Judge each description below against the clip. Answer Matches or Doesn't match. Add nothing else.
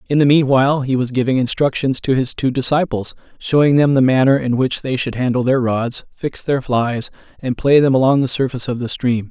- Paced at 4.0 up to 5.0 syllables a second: Doesn't match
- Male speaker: Matches